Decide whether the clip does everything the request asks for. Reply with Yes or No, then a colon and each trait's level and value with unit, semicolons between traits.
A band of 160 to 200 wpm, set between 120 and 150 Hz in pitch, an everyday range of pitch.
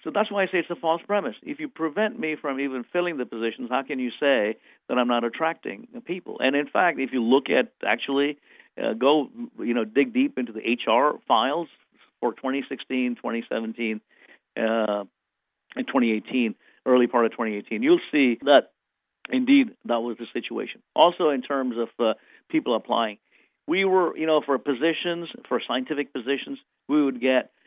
No: average, 180 wpm; medium, 140 Hz; wide, 6.4 semitones